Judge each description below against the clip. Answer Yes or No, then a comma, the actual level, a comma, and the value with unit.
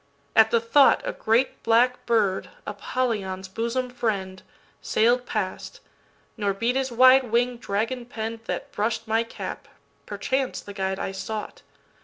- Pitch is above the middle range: Yes, high, 225 Hz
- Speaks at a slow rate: Yes, slow, 120 wpm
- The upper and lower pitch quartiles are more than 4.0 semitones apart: No, average, 3.2 semitones